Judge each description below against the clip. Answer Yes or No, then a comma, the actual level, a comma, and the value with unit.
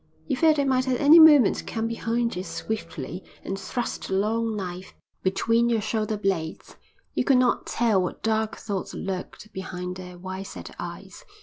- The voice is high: Yes, high, 215 Hz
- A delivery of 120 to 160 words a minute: No, average, 175 wpm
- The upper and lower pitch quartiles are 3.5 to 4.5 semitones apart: Yes, average, 4.1 semitones